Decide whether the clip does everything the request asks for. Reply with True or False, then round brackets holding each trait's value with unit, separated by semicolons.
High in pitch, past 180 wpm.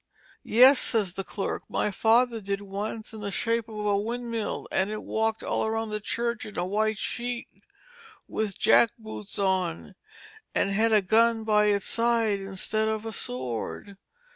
False (215 Hz; 165 wpm)